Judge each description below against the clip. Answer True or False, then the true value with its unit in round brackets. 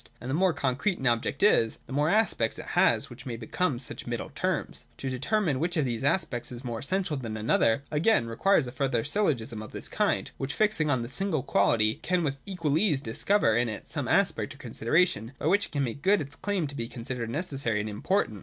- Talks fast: True (225 wpm)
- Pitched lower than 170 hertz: True (135 Hz)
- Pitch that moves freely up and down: True (6.9 semitones)